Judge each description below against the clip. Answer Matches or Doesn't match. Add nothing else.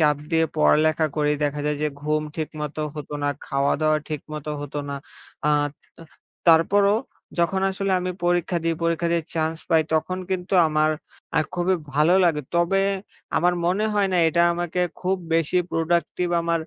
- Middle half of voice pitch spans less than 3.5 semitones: Matches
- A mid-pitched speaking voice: Matches